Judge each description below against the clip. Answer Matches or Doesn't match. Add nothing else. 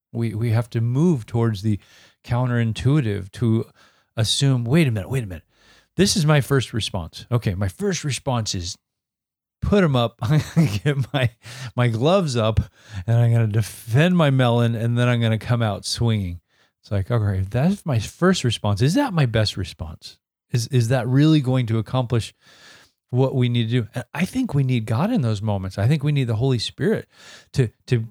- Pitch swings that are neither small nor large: Matches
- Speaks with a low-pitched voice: Matches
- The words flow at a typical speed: Matches